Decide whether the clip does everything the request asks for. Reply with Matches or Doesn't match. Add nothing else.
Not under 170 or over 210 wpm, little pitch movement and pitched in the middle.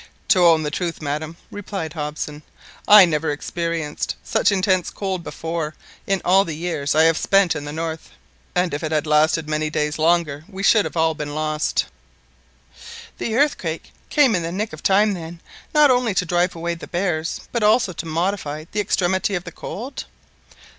Doesn't match